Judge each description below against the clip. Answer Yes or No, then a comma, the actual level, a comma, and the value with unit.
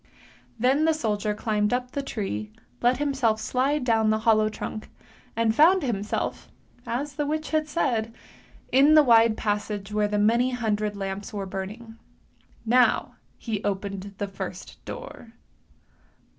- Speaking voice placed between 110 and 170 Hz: No, high, 225 Hz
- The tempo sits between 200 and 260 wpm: No, average, 145 wpm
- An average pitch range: Yes, average, 3.7 semitones